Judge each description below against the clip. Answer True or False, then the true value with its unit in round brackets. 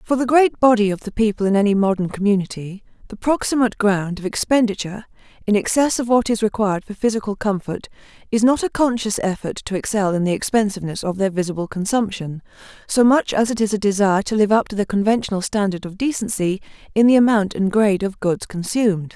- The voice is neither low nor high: False (210 Hz)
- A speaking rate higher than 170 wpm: True (195 wpm)